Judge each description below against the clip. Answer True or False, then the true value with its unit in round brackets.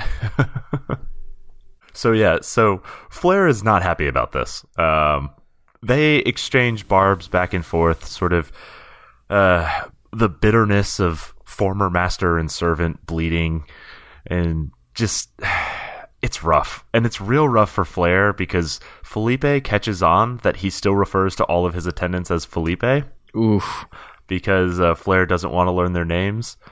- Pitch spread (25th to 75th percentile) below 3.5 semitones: False (4.2 semitones)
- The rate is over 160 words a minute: False (140 wpm)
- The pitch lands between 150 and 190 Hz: False (90 Hz)